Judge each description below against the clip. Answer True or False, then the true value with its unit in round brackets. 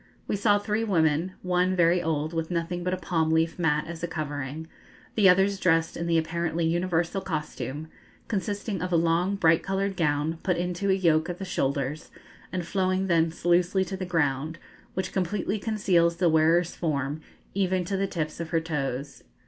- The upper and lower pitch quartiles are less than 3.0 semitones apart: True (2.6 semitones)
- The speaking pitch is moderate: True (170 Hz)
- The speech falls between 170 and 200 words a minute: True (180 wpm)